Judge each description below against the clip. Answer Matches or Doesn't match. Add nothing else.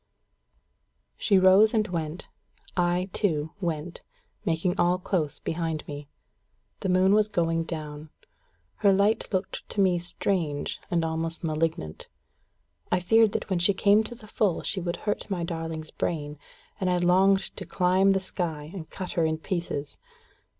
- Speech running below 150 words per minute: Doesn't match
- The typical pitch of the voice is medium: Matches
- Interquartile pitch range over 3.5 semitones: Doesn't match